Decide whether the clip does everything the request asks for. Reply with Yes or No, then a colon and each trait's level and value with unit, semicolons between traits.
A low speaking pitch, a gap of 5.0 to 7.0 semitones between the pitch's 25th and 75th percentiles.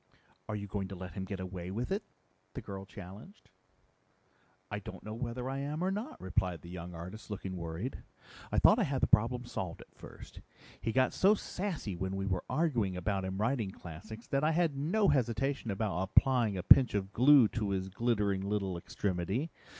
Yes: low, 105 Hz; wide, 5.6 semitones